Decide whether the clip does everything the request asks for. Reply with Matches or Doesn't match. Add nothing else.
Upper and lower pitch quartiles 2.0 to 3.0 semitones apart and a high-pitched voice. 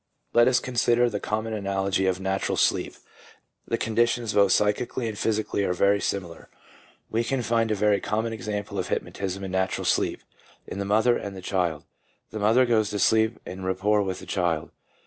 Doesn't match